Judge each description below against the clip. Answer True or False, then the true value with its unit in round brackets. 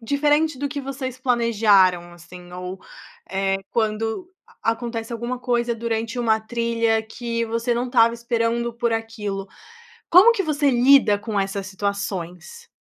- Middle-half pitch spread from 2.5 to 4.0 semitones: True (3.1 semitones)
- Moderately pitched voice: False (230 Hz)